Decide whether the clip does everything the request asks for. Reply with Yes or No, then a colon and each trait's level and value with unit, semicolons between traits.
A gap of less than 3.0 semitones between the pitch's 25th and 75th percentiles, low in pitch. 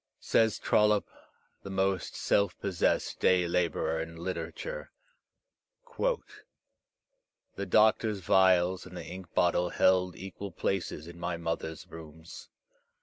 Yes: narrow, 2.4 semitones; very low, 90 Hz